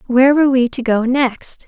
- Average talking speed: No, fast, 215 wpm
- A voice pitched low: No, very high, 255 Hz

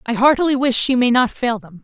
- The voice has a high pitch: Yes, very high, 250 Hz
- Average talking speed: No, fast, 260 wpm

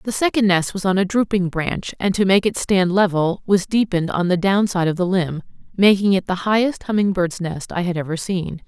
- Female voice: Yes, female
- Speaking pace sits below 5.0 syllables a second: No, 5.3 syllables/s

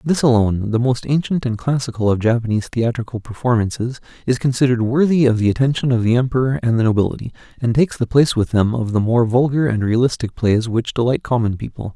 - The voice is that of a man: Yes, male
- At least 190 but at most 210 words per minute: Yes, average, 200 wpm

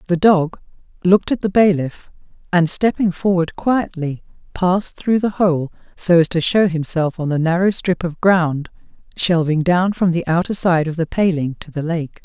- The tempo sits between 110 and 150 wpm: No, average, 180 wpm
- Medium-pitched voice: Yes, medium, 175 Hz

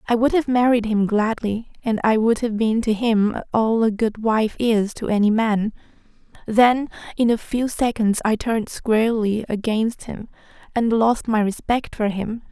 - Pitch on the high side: Yes, high, 225 Hz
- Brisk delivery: No, average, 175 wpm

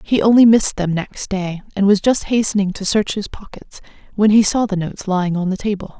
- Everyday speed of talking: No, fast, 230 wpm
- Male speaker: No, female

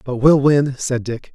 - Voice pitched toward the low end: Yes, low, 130 Hz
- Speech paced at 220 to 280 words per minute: Yes, fast, 225 wpm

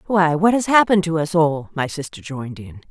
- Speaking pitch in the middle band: Yes, medium, 165 Hz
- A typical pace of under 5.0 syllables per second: No, 5.7 syllables/s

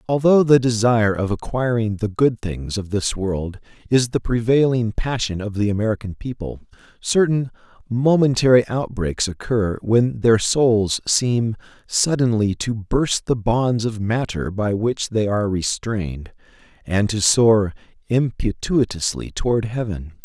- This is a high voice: No, low, 110 Hz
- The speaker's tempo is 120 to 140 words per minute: Yes, slow, 135 wpm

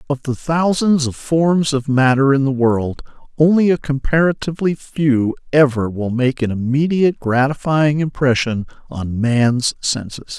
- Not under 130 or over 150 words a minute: Yes, average, 140 wpm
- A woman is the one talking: No, male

